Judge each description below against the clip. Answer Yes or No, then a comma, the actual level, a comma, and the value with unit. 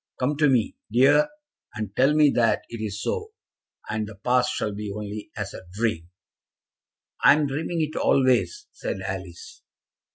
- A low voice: Yes, low, 125 Hz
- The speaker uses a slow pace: No, average, 160 wpm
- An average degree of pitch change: No, wide, 6.0 semitones